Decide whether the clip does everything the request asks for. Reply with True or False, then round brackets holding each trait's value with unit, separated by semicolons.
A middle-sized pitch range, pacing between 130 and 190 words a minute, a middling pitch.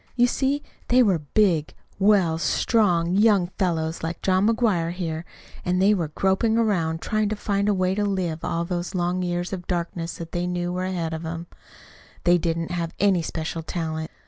True (3.1 semitones; 185 wpm; 175 Hz)